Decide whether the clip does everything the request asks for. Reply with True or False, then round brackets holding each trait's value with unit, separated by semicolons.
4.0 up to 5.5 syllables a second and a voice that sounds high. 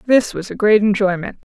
True (5.3 syllables/s; 205 Hz)